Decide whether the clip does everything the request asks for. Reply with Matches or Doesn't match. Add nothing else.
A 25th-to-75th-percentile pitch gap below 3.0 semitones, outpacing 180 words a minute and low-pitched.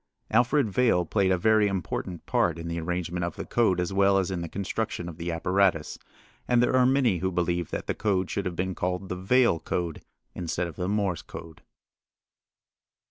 Matches